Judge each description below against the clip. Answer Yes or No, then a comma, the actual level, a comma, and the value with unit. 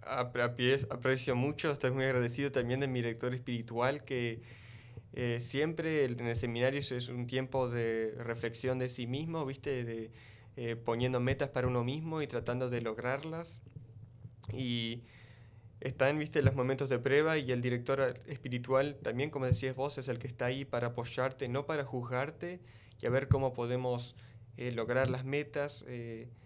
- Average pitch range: No, narrow, 2.2 semitones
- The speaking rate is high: No, average, 170 wpm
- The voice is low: Yes, low, 125 Hz